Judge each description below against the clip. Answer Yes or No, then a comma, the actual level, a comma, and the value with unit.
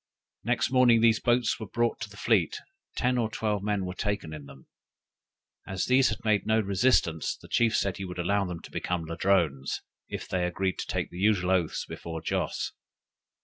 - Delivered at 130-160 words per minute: No, average, 190 wpm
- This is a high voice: No, low, 100 Hz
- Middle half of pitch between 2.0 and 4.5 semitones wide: Yes, average, 4.2 semitones